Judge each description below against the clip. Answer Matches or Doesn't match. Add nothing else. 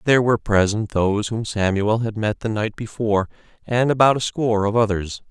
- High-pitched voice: Doesn't match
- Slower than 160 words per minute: Doesn't match